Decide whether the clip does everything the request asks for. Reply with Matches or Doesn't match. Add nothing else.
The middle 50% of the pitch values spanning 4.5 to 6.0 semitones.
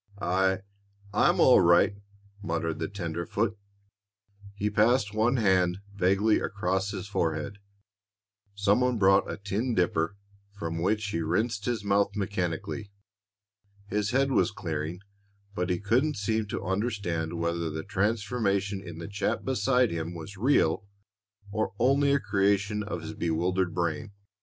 Doesn't match